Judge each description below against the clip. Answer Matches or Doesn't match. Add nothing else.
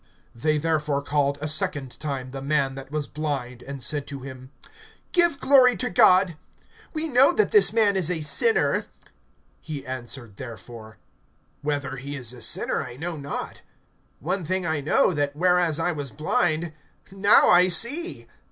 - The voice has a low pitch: Doesn't match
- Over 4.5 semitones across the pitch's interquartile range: Matches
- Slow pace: Doesn't match